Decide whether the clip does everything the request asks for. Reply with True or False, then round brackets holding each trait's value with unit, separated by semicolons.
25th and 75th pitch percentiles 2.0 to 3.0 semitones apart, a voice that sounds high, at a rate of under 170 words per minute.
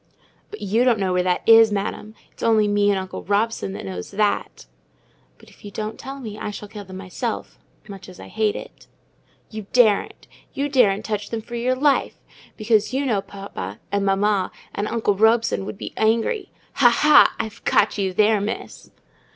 False (2.5 semitones; 210 Hz; 185 wpm)